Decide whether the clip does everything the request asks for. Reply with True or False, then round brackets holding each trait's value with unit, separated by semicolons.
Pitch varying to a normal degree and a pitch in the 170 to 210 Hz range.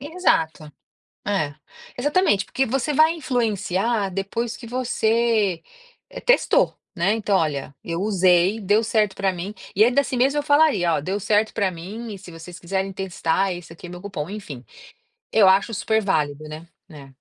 True (4.7 semitones; 200 Hz)